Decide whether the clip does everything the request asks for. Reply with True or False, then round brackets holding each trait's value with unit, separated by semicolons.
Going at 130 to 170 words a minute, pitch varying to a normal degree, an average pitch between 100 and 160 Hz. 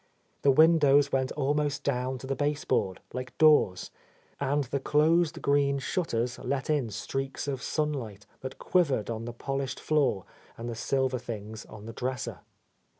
True (150 wpm; 3.4 semitones; 135 Hz)